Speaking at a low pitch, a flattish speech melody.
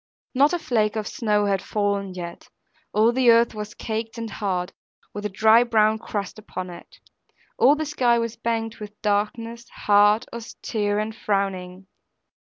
No: high, 215 Hz; narrow, 2.3 semitones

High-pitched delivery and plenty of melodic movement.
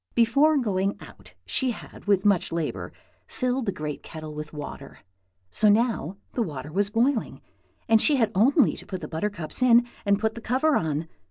Yes: high, 210 Hz; wide, 6.5 semitones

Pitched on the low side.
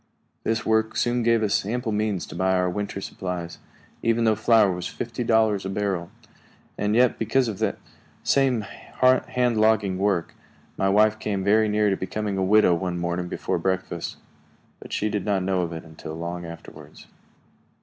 Yes: low, 105 Hz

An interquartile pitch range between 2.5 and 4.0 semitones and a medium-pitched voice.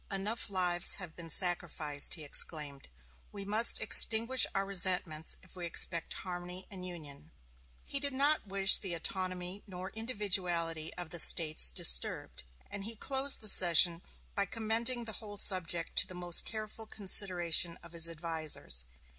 Yes: average, 3.6 semitones; medium, 180 Hz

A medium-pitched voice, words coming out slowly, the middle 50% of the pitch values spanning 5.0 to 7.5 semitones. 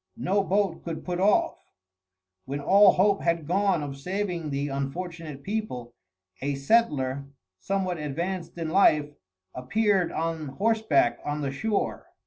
Yes: medium, 170 Hz; slow, 130 wpm; wide, 5.6 semitones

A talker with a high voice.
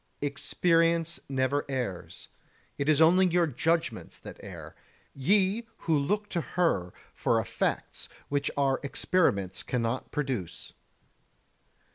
No: medium, 145 Hz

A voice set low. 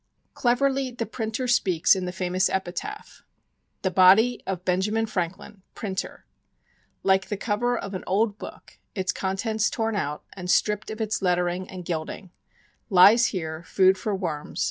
No: high, 195 Hz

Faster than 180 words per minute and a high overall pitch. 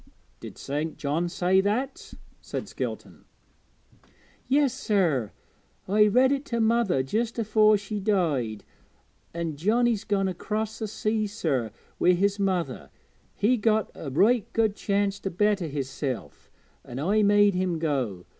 No: slow, 135 wpm; high, 200 Hz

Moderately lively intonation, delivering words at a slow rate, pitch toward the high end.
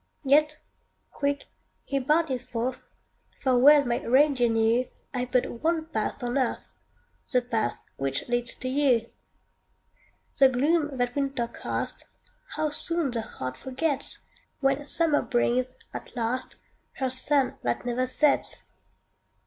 Yes: average, 3.1 semitones; slow, 130 wpm; very high, 260 Hz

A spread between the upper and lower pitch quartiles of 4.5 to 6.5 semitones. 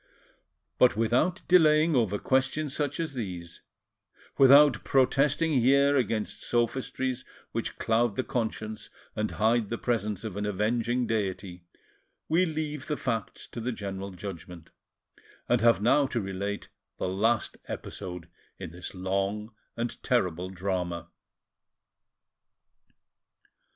Yes: average, 5.1 semitones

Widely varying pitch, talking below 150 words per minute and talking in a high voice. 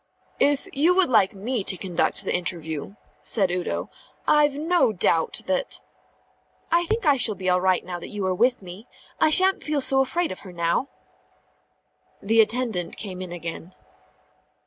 No: wide, 7.5 semitones; average, 170 wpm; high, 205 Hz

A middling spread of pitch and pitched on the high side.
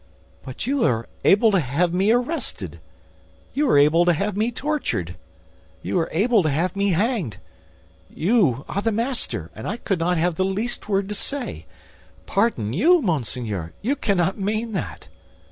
No: wide, 6.7 semitones; high, 195 Hz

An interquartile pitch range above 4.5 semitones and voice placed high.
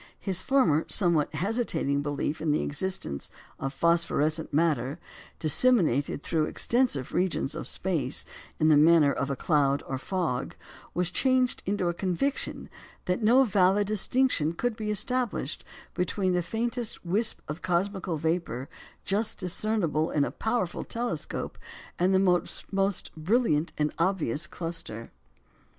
No: average, 5.2 semitones; medium, 175 Hz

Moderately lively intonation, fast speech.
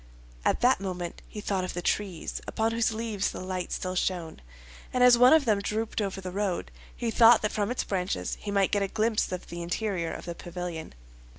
Yes: average, 3.6 semitones; fast, 215 wpm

